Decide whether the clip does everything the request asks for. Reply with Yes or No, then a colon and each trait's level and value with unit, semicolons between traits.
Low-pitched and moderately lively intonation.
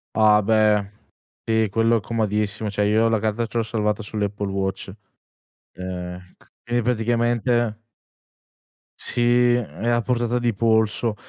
No: low, 110 Hz; narrow, 2.1 semitones